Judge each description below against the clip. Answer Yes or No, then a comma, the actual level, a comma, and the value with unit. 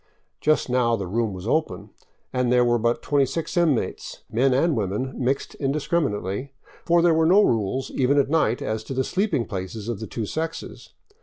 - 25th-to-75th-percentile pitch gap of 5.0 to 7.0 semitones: Yes, wide, 5.5 semitones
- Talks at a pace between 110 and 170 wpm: No, average, 180 wpm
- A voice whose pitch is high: No, low, 125 Hz